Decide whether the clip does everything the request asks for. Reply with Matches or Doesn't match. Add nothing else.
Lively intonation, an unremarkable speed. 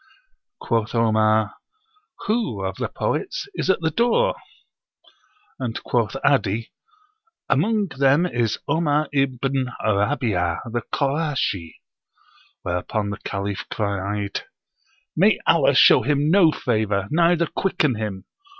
Doesn't match